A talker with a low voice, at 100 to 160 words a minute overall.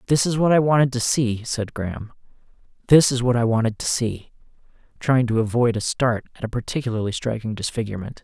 No: low, 120 Hz; average, 190 wpm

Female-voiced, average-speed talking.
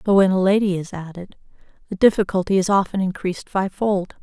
Yes: female; average, 170 wpm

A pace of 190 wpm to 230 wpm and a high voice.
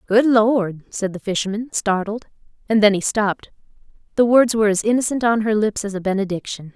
No: average, 180 wpm; high, 210 Hz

